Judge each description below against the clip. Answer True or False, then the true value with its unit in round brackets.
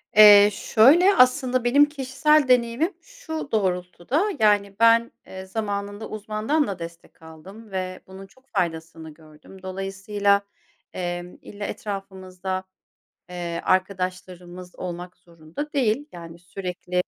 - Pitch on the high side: True (195 Hz)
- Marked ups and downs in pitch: False (4.4 semitones)